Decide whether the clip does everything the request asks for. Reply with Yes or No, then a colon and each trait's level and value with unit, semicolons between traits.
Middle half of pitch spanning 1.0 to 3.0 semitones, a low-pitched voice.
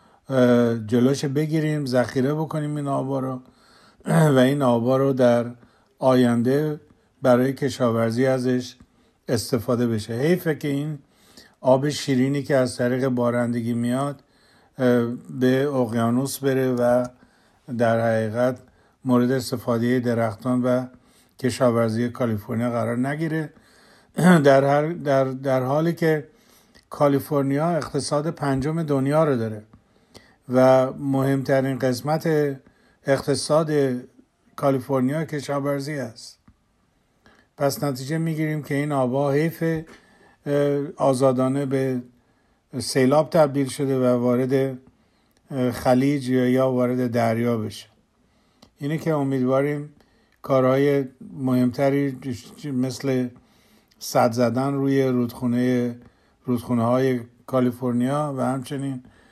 Yes: narrow, 2.4 semitones; low, 130 Hz